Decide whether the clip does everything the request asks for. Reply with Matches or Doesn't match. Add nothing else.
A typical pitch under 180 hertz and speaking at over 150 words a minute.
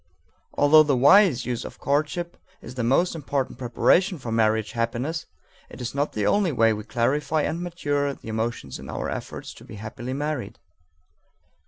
Matches